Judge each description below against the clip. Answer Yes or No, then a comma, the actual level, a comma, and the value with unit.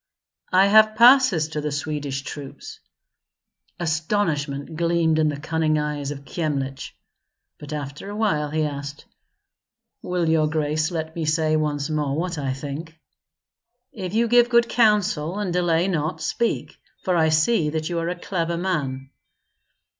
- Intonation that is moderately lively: Yes, average, 3.2 semitones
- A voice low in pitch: No, medium, 160 Hz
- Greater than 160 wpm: No, average, 150 wpm